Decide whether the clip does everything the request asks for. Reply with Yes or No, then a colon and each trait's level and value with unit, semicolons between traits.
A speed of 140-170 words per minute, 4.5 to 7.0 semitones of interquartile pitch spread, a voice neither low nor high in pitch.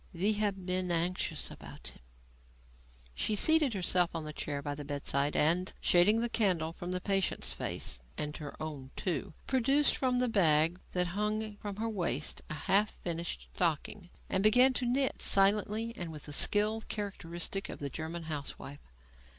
Yes: average, 165 wpm; average, 5.1 semitones; medium, 180 Hz